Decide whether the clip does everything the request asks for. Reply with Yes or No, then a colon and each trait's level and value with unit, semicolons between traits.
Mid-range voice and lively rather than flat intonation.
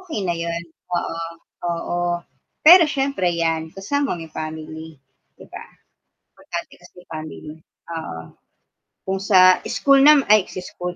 Yes: medium, 175 Hz; wide, 8.7 semitones